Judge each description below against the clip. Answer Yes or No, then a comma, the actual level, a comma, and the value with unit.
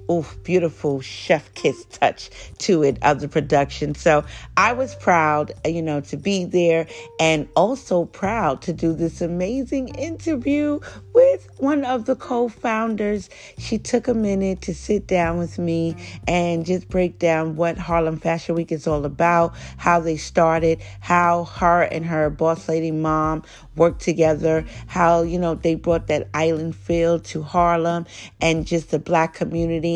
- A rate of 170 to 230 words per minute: No, average, 160 wpm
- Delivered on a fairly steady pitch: Yes, narrow, 2.3 semitones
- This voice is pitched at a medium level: Yes, medium, 170 Hz